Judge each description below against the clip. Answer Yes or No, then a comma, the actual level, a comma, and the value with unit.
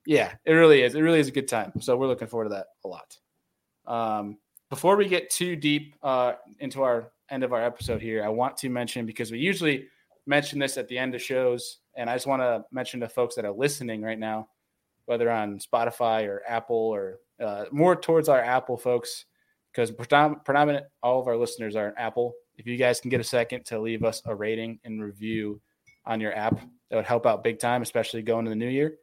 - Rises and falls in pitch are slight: No, average, 3.5 semitones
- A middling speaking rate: No, fast, 225 wpm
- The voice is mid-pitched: No, low, 120 Hz